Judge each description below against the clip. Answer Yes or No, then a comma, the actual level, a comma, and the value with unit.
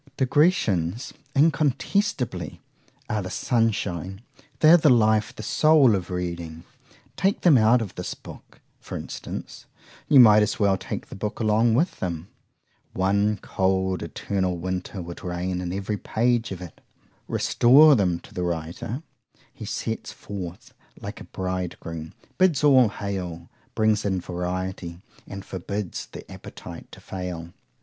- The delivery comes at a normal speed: No, slow, 125 wpm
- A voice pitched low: Yes, low, 100 Hz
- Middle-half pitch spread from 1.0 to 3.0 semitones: No, average, 5.0 semitones